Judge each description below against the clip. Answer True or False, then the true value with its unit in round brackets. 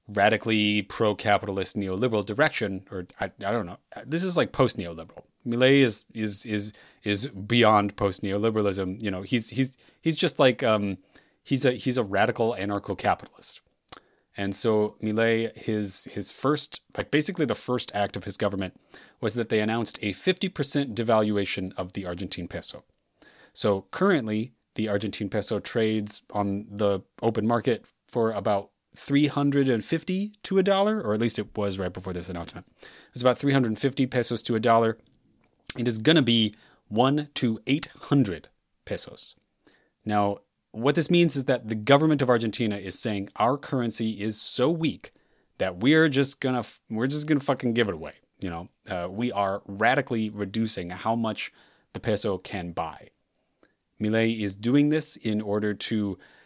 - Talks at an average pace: True (160 wpm)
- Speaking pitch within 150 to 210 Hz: False (110 Hz)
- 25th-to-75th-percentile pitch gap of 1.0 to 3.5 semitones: False (4.3 semitones)